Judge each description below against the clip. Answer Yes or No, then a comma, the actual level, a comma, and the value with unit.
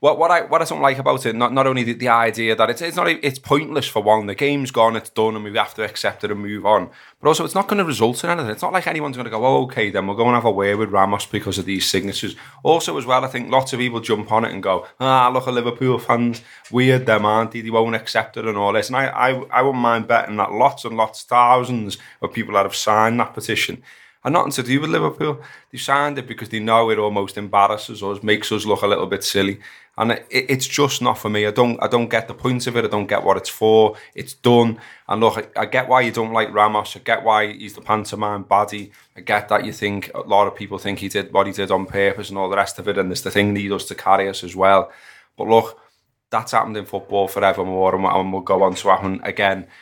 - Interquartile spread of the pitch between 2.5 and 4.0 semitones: Yes, average, 3.7 semitones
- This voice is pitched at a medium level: No, low, 110 Hz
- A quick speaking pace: Yes, fast, 275 wpm